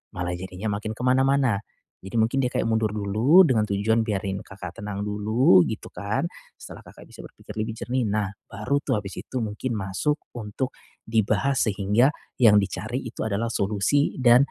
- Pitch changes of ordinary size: Yes, average, 3.4 semitones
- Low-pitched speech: Yes, low, 110 Hz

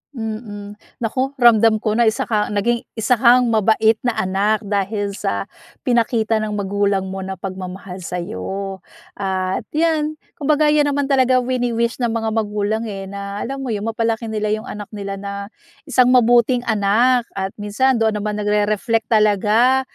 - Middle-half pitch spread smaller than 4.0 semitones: Yes, average, 3.1 semitones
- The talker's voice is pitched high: Yes, high, 220 Hz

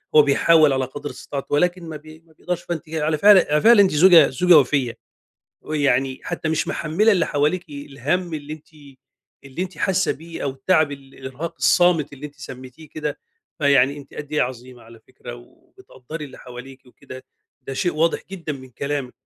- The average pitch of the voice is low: No, medium, 150 Hz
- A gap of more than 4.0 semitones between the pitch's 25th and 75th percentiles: No, average, 3.7 semitones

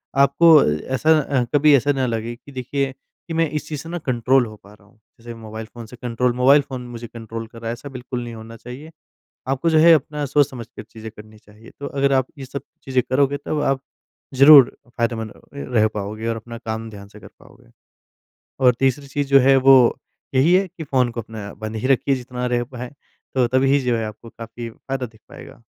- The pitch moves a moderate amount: Yes, average, 3.3 semitones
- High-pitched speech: No, low, 125 Hz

